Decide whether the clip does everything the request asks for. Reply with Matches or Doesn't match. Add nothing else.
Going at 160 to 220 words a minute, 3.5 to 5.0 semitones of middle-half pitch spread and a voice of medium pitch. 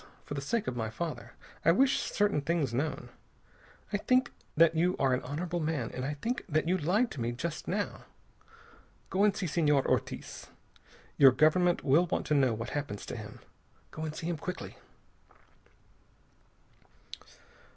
Matches